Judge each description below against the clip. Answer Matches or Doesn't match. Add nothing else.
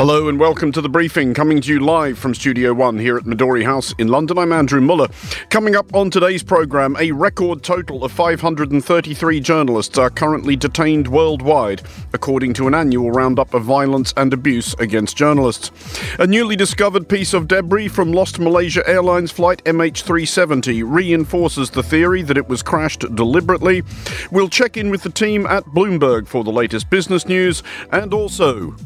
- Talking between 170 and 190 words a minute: Matches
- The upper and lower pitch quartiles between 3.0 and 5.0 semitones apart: Doesn't match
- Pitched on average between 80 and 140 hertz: Doesn't match